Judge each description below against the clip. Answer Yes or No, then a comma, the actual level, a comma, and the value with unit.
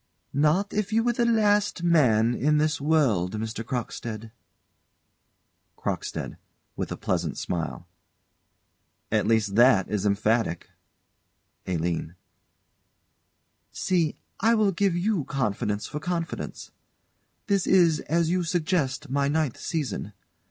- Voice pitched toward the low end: No, medium, 150 Hz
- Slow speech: Yes, slow, 115 wpm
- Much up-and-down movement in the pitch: Yes, wide, 8.1 semitones